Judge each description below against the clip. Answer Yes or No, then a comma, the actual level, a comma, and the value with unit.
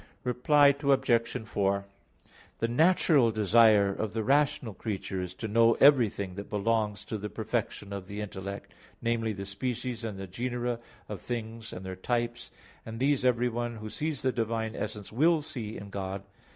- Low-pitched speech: Yes, low, 115 Hz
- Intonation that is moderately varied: Yes, average, 3.3 semitones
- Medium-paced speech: Yes, average, 165 wpm